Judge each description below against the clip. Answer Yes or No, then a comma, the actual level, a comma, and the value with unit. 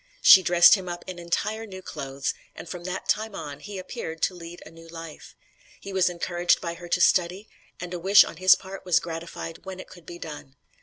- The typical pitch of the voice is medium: Yes, medium, 175 Hz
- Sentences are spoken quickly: Yes, fast, 220 wpm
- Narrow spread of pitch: Yes, narrow, 2.1 semitones